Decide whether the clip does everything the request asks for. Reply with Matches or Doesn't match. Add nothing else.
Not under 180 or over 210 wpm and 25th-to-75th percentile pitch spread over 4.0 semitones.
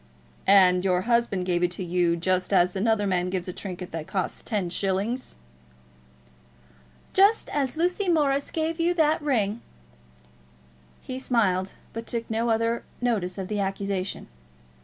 Doesn't match